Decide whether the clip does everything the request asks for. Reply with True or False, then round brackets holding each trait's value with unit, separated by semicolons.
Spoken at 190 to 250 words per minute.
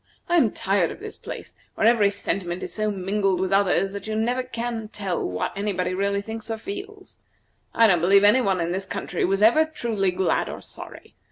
True (205 wpm)